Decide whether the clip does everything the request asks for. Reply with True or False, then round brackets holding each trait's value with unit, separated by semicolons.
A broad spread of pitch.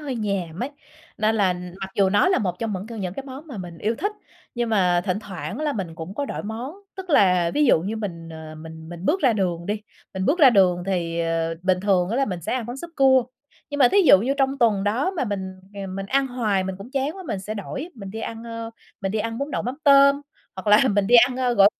True (5.7 semitones)